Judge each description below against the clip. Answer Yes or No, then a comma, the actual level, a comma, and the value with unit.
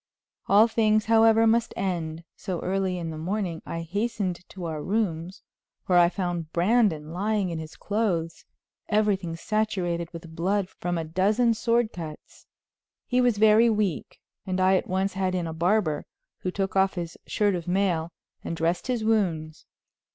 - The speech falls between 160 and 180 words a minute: Yes, average, 165 wpm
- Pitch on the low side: No, medium, 185 Hz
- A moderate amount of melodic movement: Yes, average, 4.1 semitones